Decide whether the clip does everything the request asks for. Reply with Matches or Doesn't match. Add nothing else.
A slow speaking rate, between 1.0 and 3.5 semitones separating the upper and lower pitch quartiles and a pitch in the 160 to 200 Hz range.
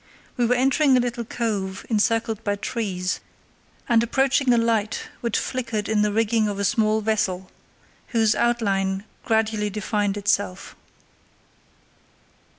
Doesn't match